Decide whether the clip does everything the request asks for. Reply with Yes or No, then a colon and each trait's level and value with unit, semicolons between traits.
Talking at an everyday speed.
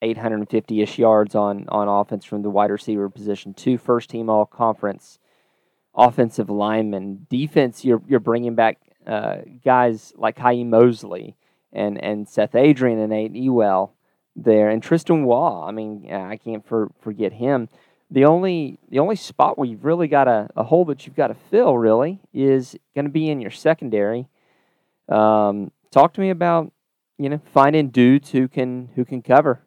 Yes: average, 170 wpm